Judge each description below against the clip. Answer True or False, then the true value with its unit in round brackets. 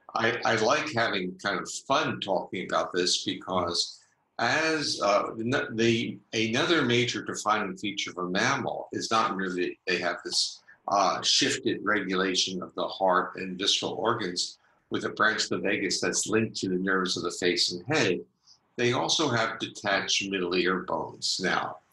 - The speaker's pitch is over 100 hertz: False (95 Hz)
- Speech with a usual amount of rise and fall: True (3.9 semitones)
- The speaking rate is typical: True (165 wpm)